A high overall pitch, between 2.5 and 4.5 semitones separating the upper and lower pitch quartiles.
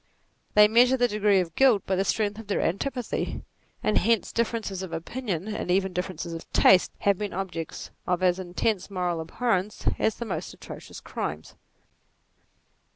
Yes: high, 195 Hz; average, 3.4 semitones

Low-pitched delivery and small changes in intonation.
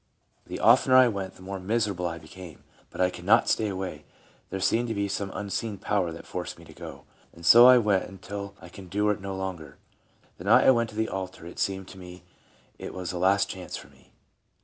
Yes: very low, 95 Hz; narrow, 2.3 semitones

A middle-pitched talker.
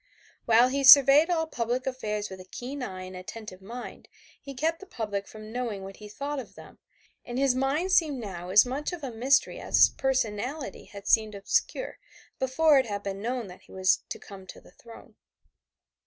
No: high, 240 Hz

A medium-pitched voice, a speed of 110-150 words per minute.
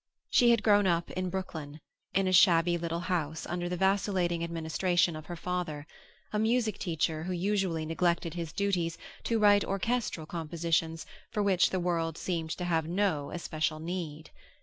No: medium, 175 Hz; average, 165 wpm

